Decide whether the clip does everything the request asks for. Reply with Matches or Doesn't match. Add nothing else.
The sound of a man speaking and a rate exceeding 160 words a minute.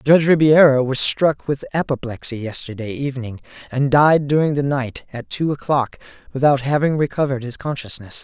Doesn't match